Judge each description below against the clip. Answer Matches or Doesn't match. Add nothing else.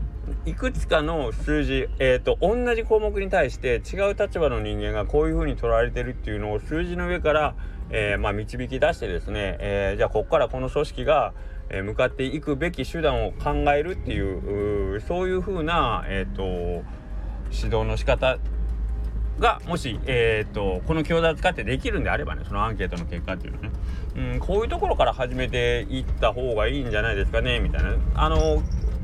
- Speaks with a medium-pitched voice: Doesn't match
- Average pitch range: Doesn't match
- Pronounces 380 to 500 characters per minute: Matches